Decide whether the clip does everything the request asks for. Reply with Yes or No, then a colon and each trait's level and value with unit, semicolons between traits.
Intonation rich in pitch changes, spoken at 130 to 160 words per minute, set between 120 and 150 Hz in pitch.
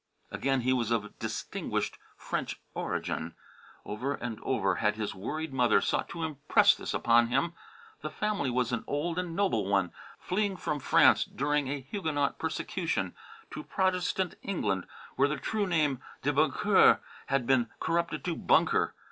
Yes: wide, 6.1 semitones; average, 155 wpm; medium, 140 Hz